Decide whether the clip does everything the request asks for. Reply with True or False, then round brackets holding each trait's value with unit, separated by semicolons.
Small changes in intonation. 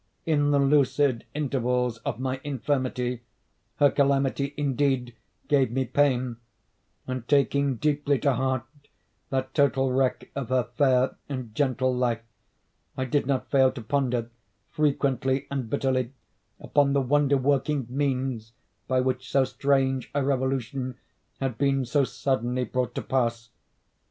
True (1.8 semitones)